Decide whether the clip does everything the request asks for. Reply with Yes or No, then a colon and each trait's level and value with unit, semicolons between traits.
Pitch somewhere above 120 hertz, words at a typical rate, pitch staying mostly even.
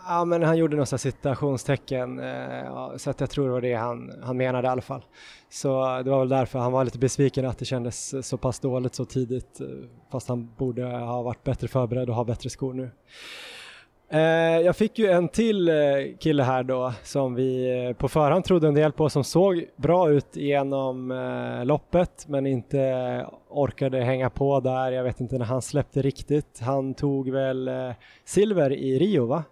Yes: low, 130 Hz; average, 180 wpm; narrow, 2.1 semitones